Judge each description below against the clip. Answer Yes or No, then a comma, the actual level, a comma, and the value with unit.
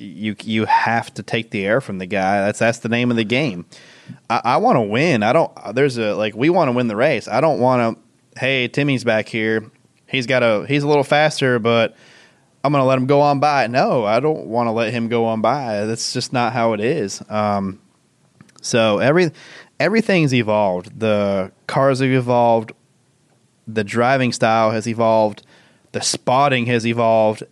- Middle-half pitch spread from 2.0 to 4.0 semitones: Yes, average, 3.4 semitones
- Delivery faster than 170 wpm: Yes, average, 195 wpm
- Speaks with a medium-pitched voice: No, low, 115 Hz